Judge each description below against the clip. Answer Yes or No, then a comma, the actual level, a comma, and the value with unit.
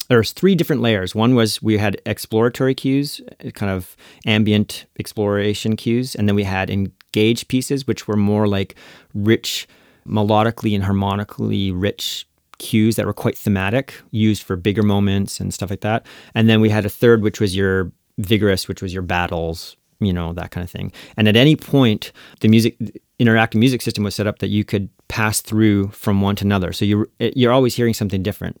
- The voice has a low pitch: Yes, low, 105 Hz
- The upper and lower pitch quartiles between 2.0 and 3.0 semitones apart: Yes, narrow, 2.5 semitones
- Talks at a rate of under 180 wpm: No, average, 195 wpm